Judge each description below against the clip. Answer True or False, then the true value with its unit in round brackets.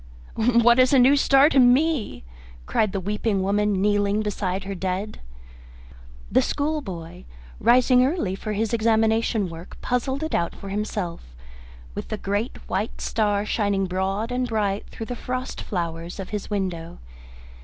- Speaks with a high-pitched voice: True (210 Hz)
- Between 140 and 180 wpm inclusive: True (150 wpm)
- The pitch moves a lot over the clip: False (4.1 semitones)